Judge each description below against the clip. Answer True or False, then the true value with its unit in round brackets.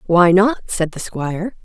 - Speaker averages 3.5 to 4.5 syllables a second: True (4.4 syllables/s)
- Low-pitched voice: False (185 Hz)